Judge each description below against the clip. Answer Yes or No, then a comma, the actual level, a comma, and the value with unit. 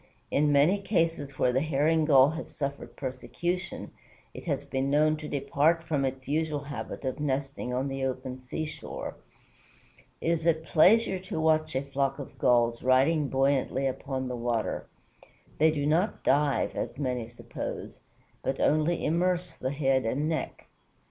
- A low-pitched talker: No, medium, 145 Hz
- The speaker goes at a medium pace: Yes, average, 155 wpm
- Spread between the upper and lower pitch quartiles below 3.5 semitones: Yes, average, 3.1 semitones